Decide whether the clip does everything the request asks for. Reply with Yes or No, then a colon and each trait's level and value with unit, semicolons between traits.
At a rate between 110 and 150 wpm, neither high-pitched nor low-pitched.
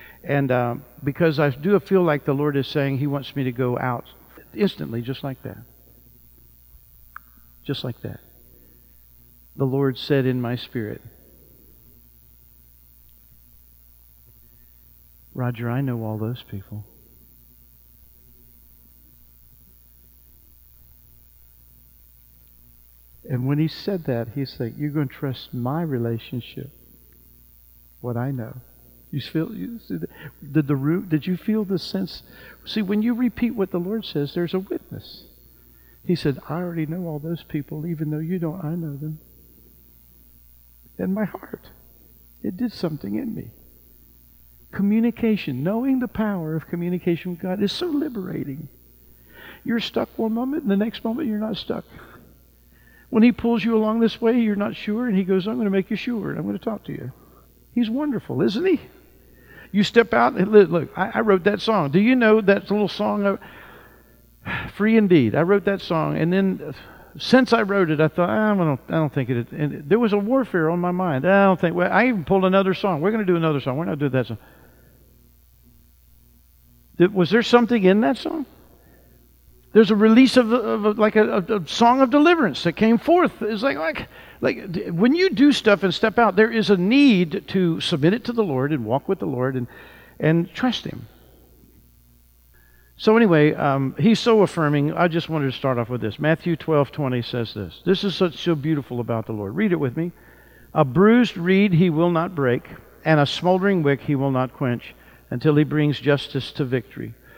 No: average, 175 wpm; medium, 150 Hz